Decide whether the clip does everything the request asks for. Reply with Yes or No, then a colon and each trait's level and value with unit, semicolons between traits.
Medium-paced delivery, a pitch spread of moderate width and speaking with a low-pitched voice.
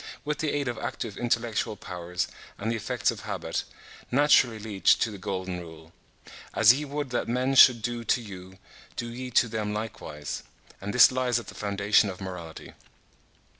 Yes: average, 175 wpm; average, 4.3 semitones; low, 110 Hz